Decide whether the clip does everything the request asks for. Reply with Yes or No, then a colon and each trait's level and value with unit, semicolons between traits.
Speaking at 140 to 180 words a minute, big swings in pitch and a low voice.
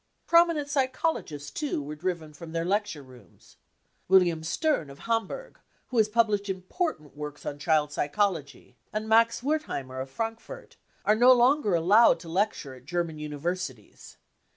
No: average, 150 wpm; wide, 7.4 semitones; medium, 185 Hz